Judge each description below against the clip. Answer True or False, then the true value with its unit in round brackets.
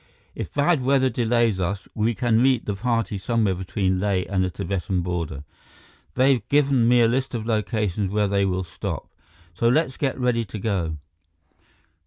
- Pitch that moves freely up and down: False (4.6 semitones)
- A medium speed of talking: True (170 wpm)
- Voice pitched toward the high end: False (110 Hz)